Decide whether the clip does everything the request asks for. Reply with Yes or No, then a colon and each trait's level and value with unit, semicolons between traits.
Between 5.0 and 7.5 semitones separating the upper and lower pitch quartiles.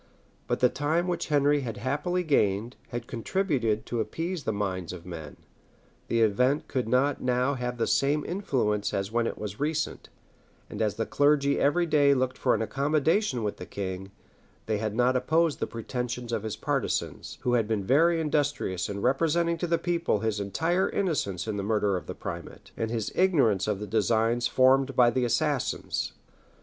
Yes: wide, 5.5 semitones